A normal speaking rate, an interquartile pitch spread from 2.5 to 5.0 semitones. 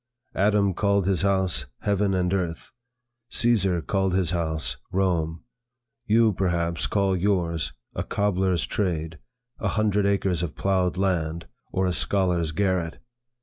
No: slow, 130 wpm; average, 2.8 semitones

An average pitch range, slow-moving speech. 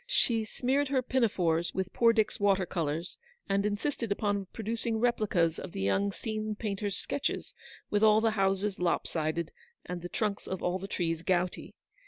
No: average, 3.8 semitones; average, 170 wpm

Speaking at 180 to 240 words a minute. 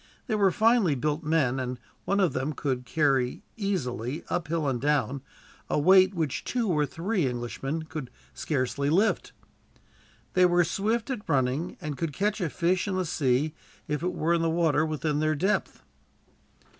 No: average, 165 wpm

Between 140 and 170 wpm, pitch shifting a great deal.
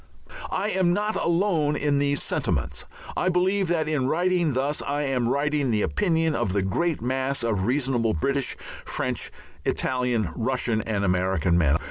Yes: average, 155 wpm; wide, 6.0 semitones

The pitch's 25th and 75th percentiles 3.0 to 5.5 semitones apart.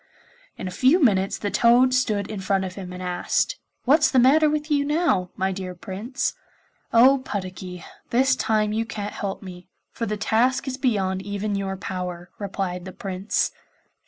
Yes: average, 5.2 semitones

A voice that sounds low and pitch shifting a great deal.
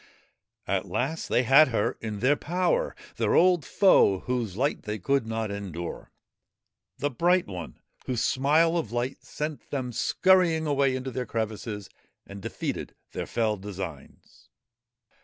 Yes: low, 125 Hz; wide, 6.3 semitones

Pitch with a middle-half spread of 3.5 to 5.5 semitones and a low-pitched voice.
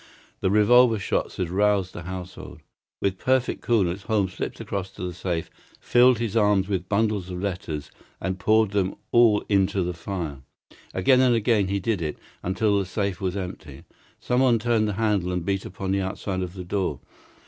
No: average, 2.8 semitones; low, 100 Hz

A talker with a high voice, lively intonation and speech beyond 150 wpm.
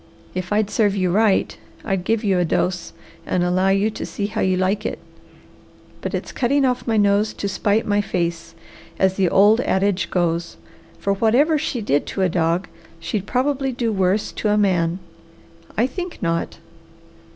No: high, 200 Hz; average, 3.2 semitones; average, 175 wpm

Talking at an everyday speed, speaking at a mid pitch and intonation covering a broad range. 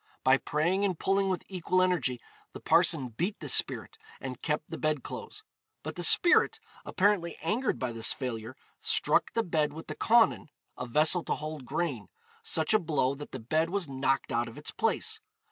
Yes: average, 185 wpm; medium, 155 Hz; wide, 5.8 semitones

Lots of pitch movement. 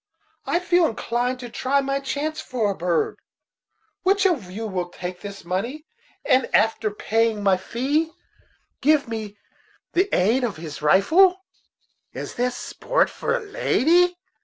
Yes: wide, 7.5 semitones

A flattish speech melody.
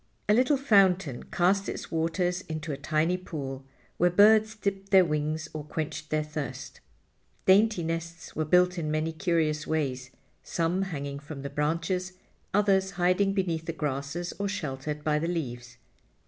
No: average, 3.8 semitones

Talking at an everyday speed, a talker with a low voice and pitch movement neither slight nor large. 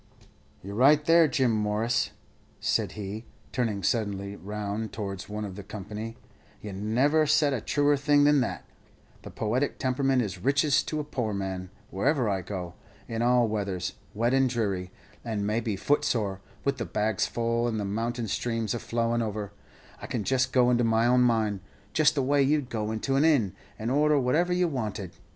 Yes: average, 180 wpm; low, 115 Hz; average, 4.3 semitones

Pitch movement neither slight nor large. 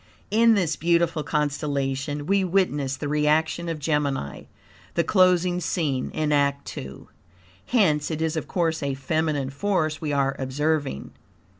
Yes: average, 3.2 semitones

